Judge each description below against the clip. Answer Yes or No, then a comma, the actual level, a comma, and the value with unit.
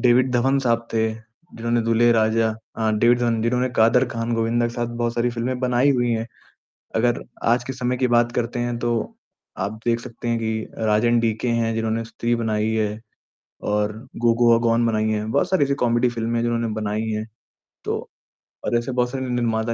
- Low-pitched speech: Yes, low, 115 Hz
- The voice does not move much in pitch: Yes, narrow, 1.4 semitones